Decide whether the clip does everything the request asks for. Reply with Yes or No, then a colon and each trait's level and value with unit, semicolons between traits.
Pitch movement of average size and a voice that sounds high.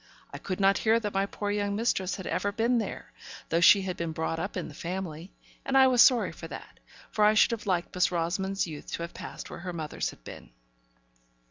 Yes: average, 3.7 semitones; high, 195 Hz